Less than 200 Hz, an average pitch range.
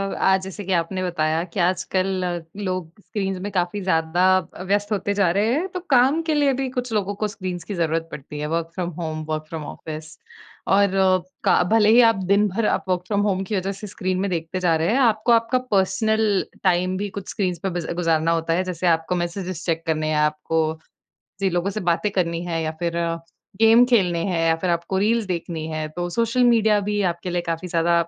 Yes: medium, 185 Hz; average, 3.6 semitones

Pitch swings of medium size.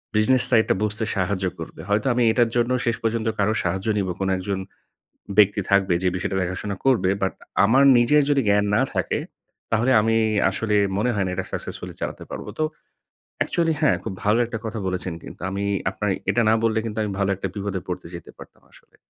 Yes: average, 3.0 semitones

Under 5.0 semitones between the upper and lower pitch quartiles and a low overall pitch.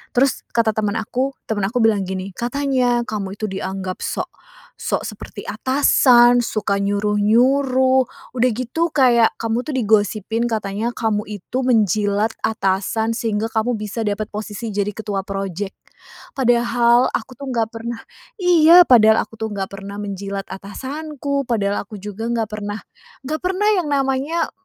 No: average, 3.7 semitones; high, 225 Hz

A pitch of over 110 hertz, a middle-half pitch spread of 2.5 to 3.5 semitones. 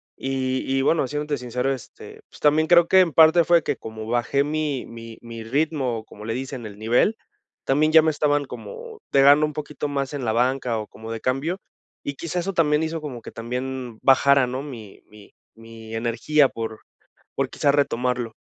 No: low, 135 Hz; average, 4.4 semitones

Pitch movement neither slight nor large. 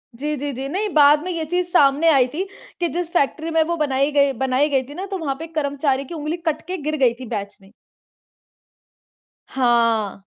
Yes: average, 3.5 semitones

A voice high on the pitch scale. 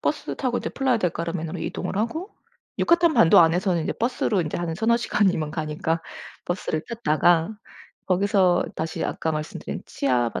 No: medium, 175 Hz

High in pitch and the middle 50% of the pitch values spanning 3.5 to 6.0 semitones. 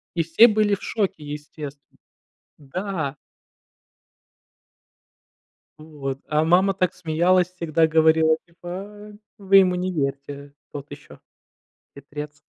No: medium, 160 Hz; average, 3.9 semitones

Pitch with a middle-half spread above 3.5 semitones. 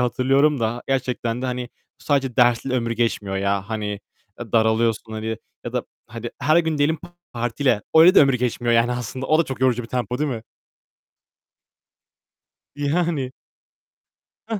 No: average, 3.2 semitones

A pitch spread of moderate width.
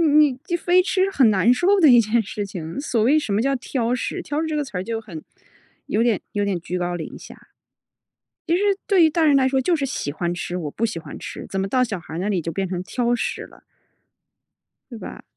No: wide, 7.4 semitones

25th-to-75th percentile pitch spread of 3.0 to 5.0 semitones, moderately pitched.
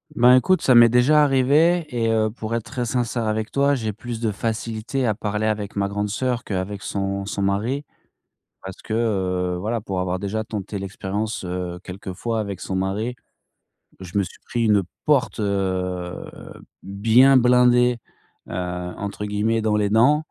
No: average, 3.6 semitones; low, 110 Hz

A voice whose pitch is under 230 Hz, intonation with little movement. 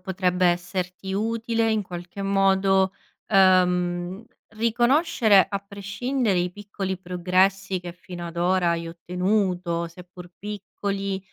Yes: high, 190 Hz; narrow, 2.0 semitones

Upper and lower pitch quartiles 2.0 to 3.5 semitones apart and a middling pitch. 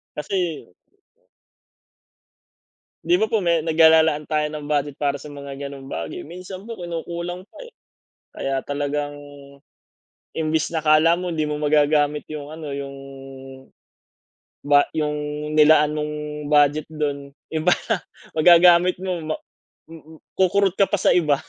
Yes: average, 2.7 semitones; medium, 155 Hz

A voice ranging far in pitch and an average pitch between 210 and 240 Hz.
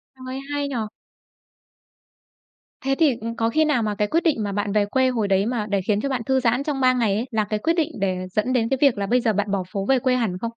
No: average, 4.3 semitones; high, 230 Hz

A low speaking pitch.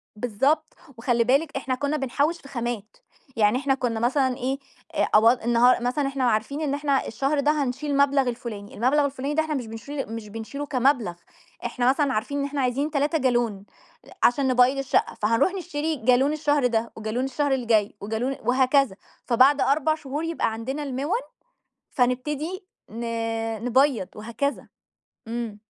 No: very high, 265 Hz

